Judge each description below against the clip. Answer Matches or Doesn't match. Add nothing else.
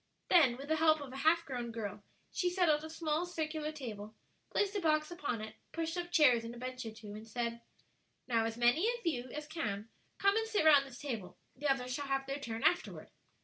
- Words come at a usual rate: Doesn't match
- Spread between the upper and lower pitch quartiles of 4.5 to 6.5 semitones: Matches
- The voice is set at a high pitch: Matches